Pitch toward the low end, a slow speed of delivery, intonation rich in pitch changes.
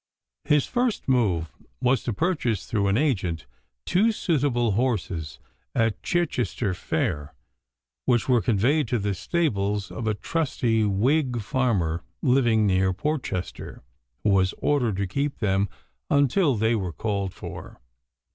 Yes: low, 115 Hz; slow, 130 wpm; wide, 5.7 semitones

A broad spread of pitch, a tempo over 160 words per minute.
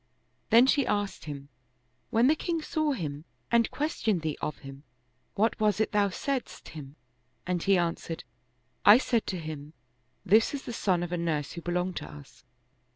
Yes: wide, 7.0 semitones; average, 195 wpm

